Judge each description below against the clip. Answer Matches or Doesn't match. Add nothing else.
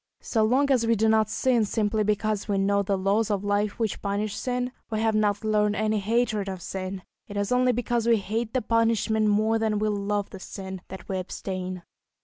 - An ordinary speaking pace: Doesn't match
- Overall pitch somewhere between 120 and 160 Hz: Doesn't match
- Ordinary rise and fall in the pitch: Doesn't match